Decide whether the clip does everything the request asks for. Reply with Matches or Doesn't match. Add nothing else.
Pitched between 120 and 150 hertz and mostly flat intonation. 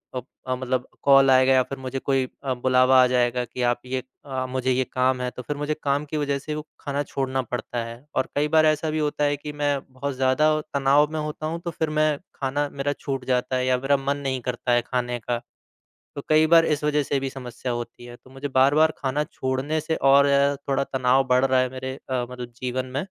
Matches